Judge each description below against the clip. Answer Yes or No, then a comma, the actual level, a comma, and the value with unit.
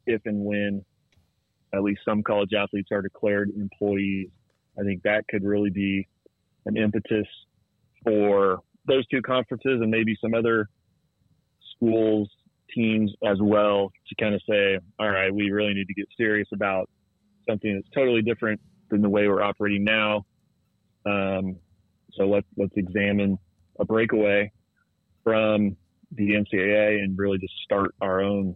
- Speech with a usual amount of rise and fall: No, narrow, 1.6 semitones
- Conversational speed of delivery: Yes, average, 145 wpm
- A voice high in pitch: No, low, 105 Hz